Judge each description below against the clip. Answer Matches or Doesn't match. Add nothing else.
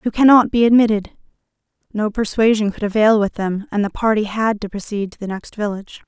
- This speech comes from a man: Doesn't match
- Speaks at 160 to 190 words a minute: Doesn't match